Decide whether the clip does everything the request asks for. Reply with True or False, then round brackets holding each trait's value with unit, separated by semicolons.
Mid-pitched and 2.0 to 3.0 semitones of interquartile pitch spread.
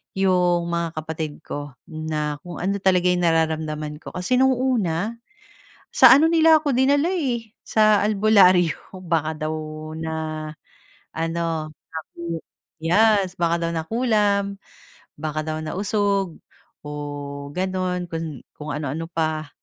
False (175 Hz; 4.1 semitones)